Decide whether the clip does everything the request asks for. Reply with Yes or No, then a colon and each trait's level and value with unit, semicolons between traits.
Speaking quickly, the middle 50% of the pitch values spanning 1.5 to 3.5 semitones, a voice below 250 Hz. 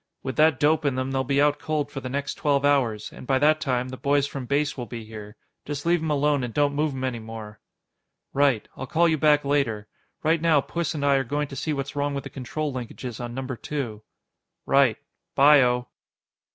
Yes: fast, 225 wpm; average, 2.7 semitones; medium, 140 Hz